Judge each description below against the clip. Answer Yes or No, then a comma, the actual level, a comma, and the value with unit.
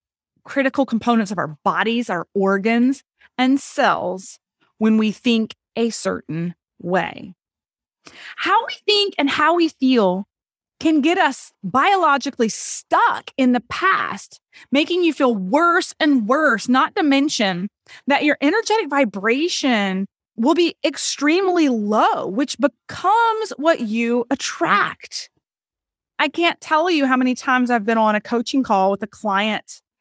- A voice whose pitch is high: Yes, very high, 260 Hz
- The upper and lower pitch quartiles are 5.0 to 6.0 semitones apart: Yes, wide, 5.6 semitones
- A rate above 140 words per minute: No, slow, 135 wpm